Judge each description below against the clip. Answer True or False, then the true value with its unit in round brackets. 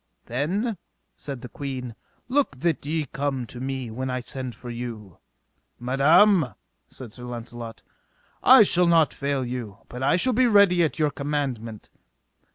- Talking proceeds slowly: False (150 wpm)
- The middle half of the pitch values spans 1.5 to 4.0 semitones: False (4.8 semitones)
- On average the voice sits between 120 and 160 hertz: True (135 Hz)